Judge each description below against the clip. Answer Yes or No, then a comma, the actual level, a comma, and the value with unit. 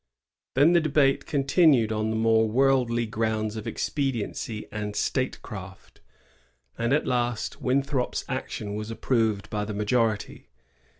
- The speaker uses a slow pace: Yes, slow, 125 wpm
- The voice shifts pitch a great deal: No, average, 3.9 semitones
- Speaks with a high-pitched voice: No, low, 115 Hz